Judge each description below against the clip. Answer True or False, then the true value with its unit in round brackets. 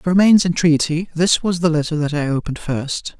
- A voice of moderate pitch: True (165 Hz)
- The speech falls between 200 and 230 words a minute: True (205 wpm)